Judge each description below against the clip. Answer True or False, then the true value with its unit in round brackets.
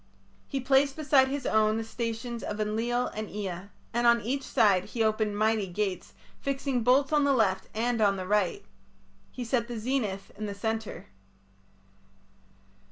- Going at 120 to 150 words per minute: False (165 wpm)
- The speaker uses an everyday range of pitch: True (3.1 semitones)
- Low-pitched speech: False (225 Hz)